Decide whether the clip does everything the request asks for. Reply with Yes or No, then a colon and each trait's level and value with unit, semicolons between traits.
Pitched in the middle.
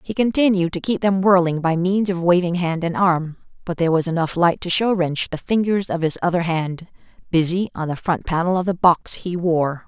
Yes: medium, 175 Hz